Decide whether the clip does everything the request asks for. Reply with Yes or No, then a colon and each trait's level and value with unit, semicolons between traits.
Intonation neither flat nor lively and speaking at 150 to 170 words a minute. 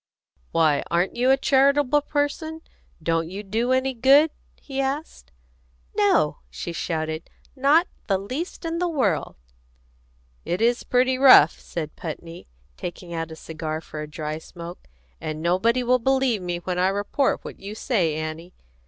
No: wide, 8.3 semitones; average, 155 wpm